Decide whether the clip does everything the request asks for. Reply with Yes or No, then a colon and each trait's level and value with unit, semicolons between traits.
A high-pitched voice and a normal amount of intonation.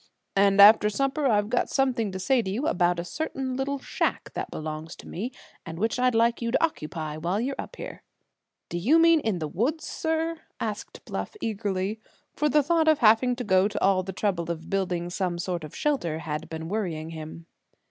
No: high, 205 Hz; wide, 7.1 semitones